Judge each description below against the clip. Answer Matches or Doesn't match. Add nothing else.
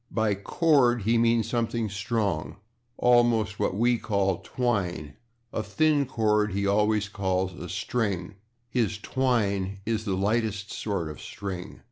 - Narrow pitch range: Doesn't match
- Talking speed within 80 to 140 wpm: Matches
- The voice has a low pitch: Matches